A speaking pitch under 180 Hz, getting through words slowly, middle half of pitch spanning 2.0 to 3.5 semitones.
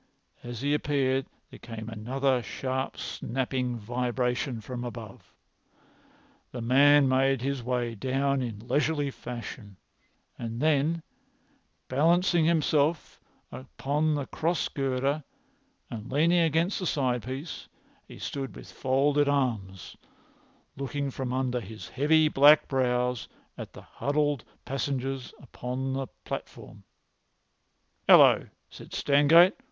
Yes: low, 135 Hz; slow, 115 wpm; average, 2.8 semitones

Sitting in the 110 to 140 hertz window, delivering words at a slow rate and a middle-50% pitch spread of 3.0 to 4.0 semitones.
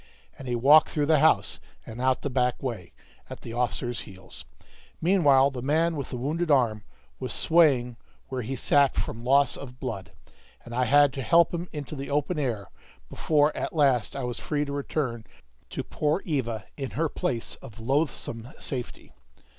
No: low, 135 Hz; average, 180 wpm; average, 3.5 semitones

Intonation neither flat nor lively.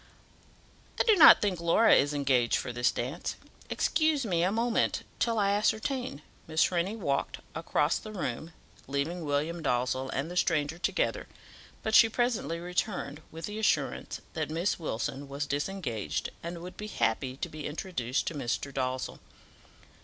No: wide, 6.2 semitones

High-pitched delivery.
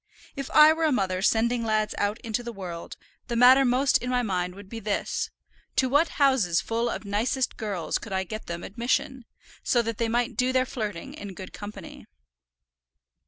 Yes: high, 230 Hz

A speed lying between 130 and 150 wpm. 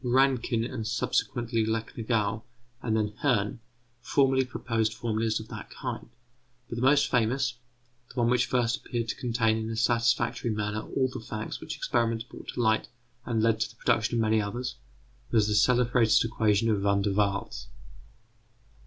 No: average, 165 wpm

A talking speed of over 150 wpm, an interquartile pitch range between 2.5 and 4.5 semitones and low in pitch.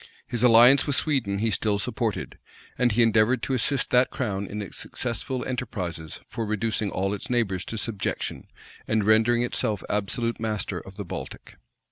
Yes: average, 165 wpm; average, 3.0 semitones; low, 115 Hz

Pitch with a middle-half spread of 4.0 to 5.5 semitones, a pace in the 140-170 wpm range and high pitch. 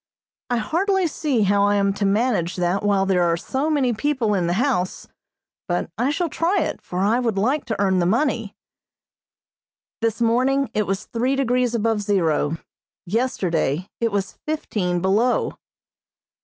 Yes: average, 4.9 semitones; average, 160 wpm; high, 215 Hz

